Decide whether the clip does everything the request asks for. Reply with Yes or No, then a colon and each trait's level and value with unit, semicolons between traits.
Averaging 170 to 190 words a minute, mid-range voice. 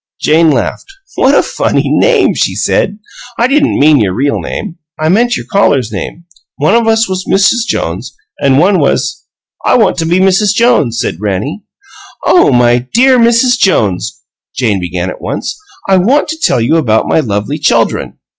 Yes: average, 180 wpm; medium, 165 Hz